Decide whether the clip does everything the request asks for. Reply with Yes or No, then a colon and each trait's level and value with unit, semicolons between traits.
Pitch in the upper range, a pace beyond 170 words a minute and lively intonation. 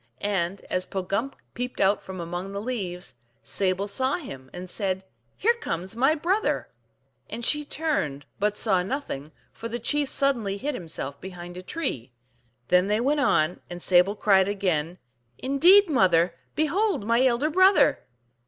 No: high, 200 Hz; average, 165 wpm; wide, 7.3 semitones